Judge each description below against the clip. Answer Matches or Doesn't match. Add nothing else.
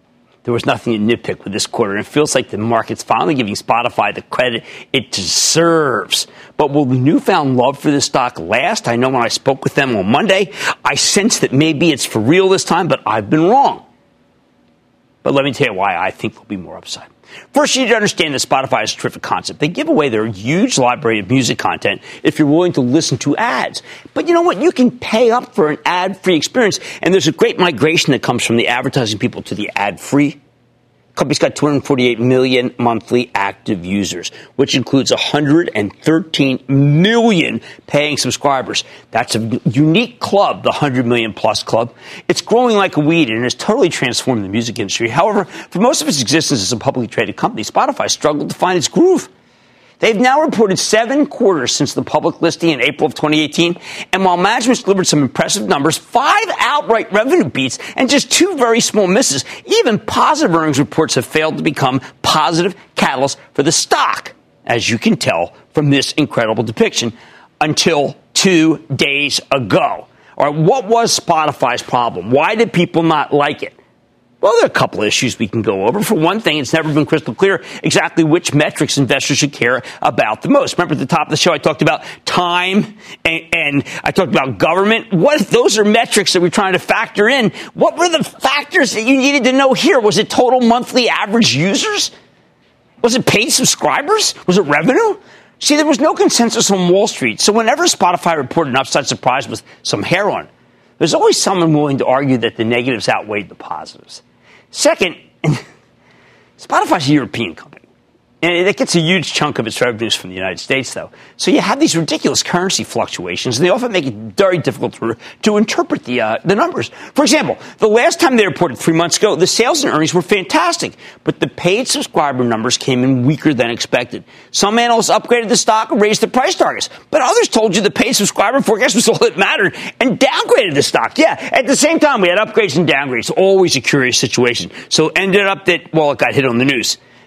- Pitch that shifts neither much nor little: Doesn't match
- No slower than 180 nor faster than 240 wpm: Matches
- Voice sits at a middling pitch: Matches